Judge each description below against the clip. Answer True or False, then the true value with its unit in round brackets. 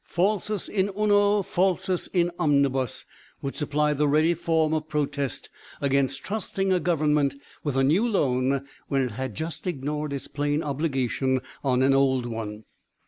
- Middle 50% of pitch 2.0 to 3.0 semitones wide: False (4.4 semitones)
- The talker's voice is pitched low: False (150 Hz)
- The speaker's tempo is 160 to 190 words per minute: False (150 wpm)